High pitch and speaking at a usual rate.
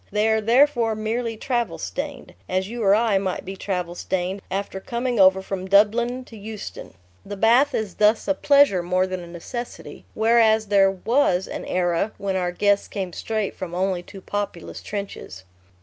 Yes: high, 200 Hz; average, 175 wpm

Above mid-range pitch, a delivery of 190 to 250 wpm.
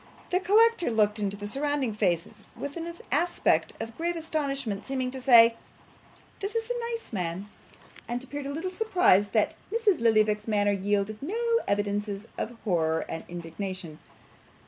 No: high, 230 Hz; average, 150 wpm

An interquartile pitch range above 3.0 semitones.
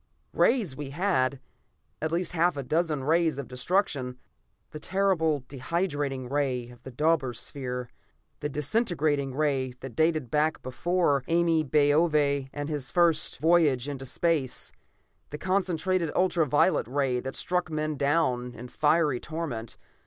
Yes: average, 4.0 semitones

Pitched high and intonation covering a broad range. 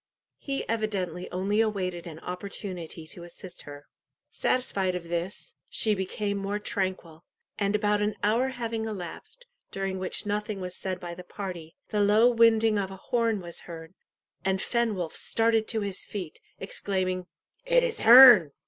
No: high, 200 Hz; average, 3.4 semitones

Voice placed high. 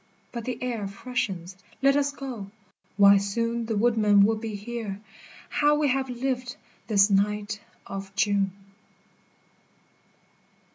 Yes: high, 220 Hz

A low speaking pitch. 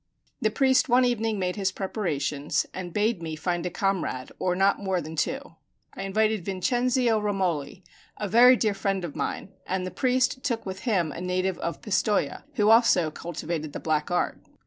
No: high, 195 Hz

